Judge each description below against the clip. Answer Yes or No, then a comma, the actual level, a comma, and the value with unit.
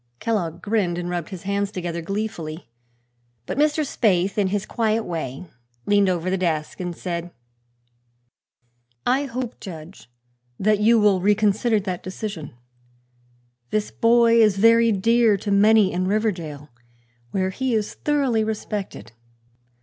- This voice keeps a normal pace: No, slow, 130 wpm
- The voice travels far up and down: No, average, 3.9 semitones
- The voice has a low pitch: No, high, 200 Hz